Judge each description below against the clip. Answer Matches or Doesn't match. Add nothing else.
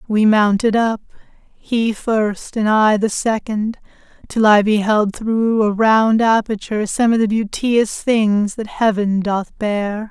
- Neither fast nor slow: Matches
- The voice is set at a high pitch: Matches